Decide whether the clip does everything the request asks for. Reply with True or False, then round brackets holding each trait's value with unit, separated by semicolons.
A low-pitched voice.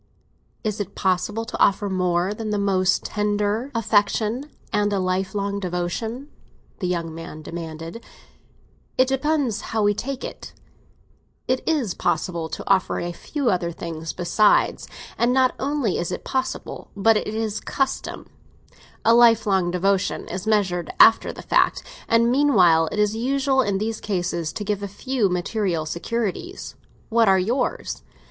False (205 Hz)